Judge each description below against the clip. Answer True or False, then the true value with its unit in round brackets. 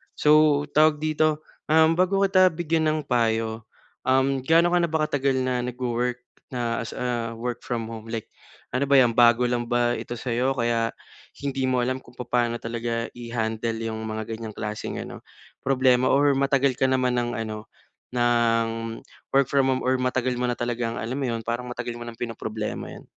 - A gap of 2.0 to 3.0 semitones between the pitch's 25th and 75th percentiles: True (2.7 semitones)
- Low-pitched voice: True (125 Hz)